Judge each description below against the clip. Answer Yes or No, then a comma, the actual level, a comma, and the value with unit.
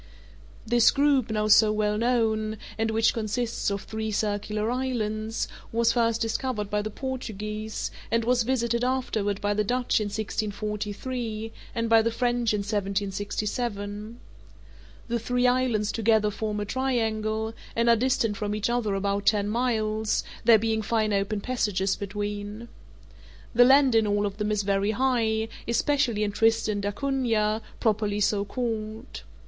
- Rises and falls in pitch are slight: Yes, narrow, 2.2 semitones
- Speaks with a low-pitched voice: No, high, 220 Hz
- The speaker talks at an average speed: Yes, average, 145 wpm